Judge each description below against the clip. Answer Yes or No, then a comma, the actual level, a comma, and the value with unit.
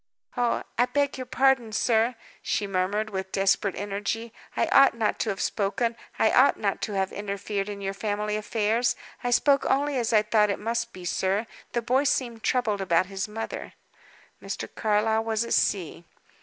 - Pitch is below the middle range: No, high, 215 Hz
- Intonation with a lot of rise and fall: No, average, 2.9 semitones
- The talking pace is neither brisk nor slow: Yes, average, 180 wpm